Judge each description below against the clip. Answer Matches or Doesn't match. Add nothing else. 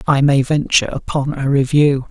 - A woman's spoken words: Doesn't match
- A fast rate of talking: Doesn't match